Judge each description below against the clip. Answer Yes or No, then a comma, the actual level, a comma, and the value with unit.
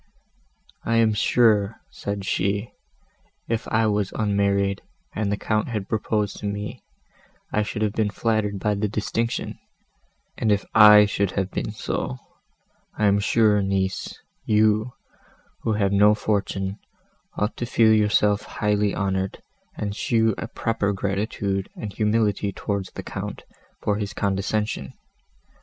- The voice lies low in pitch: Yes, low, 105 Hz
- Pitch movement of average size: No, narrow, 1.5 semitones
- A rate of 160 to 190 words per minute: No, average, 140 wpm